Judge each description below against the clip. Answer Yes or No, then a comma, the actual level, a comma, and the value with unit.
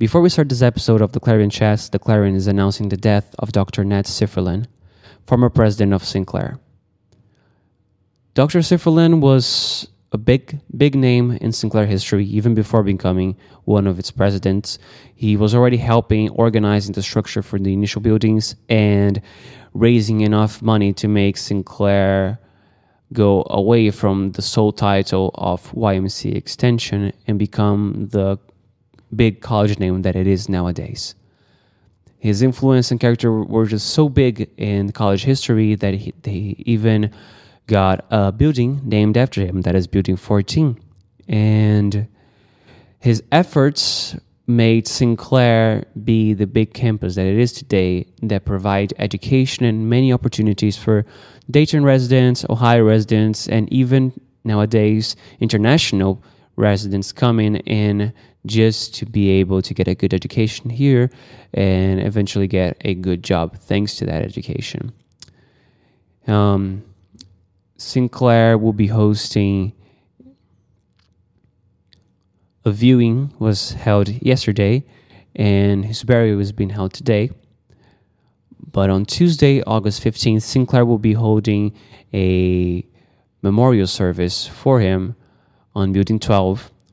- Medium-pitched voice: No, low, 105 Hz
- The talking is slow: Yes, slow, 130 wpm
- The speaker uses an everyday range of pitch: Yes, average, 3.2 semitones